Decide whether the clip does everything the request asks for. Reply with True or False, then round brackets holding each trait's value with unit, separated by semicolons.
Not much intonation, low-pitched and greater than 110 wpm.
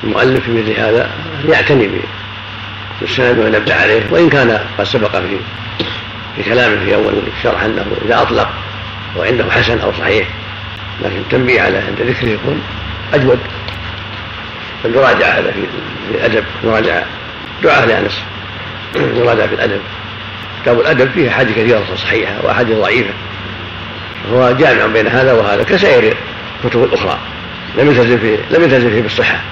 True (1.8 semitones; 105 Hz; 125 wpm)